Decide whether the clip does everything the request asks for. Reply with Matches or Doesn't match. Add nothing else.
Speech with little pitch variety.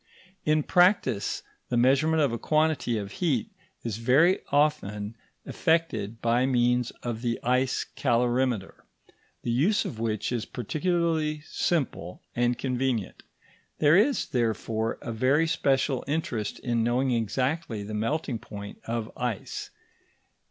Doesn't match